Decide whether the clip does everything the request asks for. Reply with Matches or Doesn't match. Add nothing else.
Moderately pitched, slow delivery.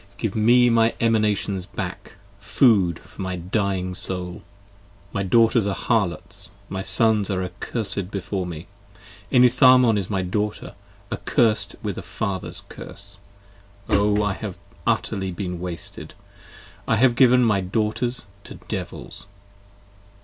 Doesn't match